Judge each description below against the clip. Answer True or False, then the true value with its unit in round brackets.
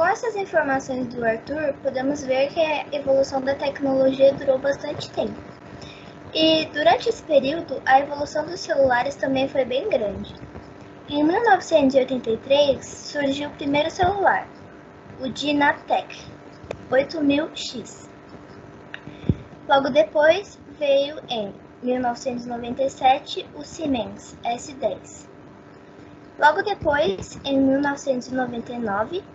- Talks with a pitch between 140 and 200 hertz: False (280 Hz)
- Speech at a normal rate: False (100 wpm)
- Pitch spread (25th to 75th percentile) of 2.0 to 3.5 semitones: True (2.6 semitones)